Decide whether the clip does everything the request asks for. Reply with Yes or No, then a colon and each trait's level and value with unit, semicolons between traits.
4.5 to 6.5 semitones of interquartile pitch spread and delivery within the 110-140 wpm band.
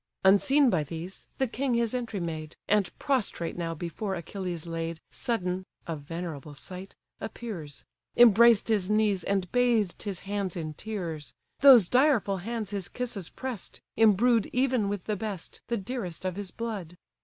No: average, 5.1 semitones; average, 155 wpm